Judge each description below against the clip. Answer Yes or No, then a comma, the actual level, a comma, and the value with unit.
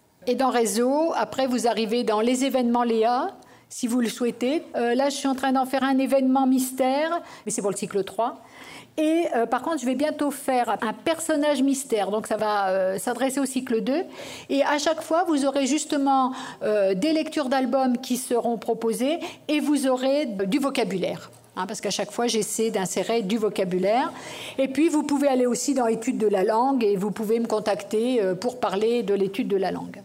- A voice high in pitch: Yes, very high, 250 Hz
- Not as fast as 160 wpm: No, average, 205 wpm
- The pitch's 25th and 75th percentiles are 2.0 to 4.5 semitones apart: Yes, average, 3.9 semitones